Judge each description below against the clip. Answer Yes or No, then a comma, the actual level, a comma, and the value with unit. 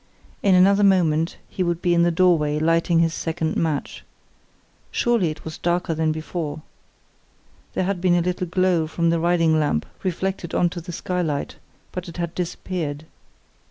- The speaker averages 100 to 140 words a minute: No, average, 165 wpm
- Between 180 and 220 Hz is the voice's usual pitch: No, medium, 170 Hz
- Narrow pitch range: Yes, narrow, 2.1 semitones